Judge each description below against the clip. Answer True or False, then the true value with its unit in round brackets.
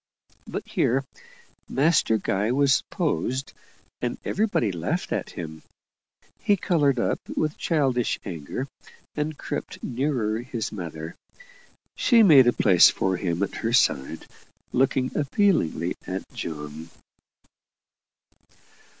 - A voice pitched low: True (120 Hz)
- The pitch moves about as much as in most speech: False (7.8 semitones)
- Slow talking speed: True (110 wpm)